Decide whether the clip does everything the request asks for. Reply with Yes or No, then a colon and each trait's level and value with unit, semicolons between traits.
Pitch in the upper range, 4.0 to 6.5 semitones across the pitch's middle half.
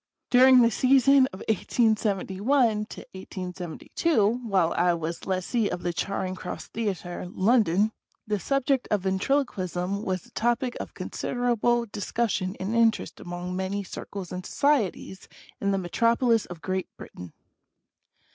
Yes: high, 205 Hz; average, 4.4 semitones